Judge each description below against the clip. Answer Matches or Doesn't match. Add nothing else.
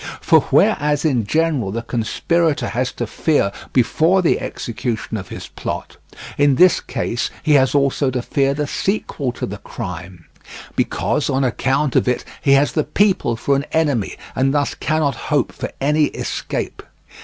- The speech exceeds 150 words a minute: Matches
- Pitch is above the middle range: Doesn't match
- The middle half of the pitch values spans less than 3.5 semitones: Doesn't match